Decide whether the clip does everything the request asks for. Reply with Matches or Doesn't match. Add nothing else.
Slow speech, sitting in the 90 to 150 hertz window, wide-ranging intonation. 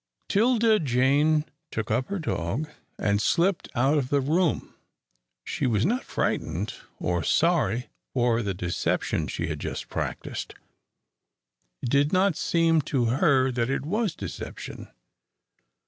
Matches